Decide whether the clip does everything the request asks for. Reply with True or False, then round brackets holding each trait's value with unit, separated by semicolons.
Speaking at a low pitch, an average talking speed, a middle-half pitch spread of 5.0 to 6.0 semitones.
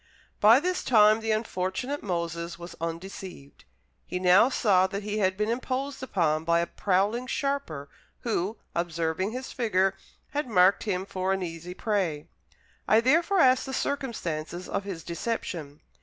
False (195 Hz; 150 wpm; 5.5 semitones)